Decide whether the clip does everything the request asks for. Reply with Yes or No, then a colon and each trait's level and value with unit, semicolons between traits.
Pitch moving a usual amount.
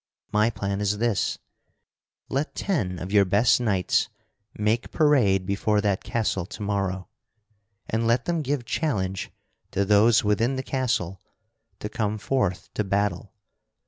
Yes: average, 3.3 semitones